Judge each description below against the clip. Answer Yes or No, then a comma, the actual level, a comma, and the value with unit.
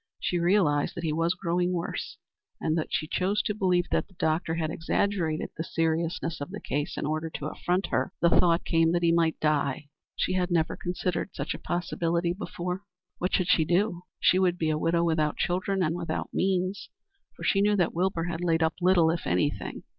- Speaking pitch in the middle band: Yes, medium, 170 Hz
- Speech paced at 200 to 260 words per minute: Yes, fast, 205 wpm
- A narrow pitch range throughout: Yes, narrow, 2.1 semitones